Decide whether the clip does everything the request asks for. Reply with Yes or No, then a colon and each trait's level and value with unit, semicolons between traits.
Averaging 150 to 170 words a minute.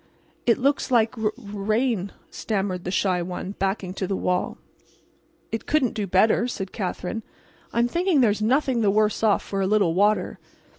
Yes: average, 165 wpm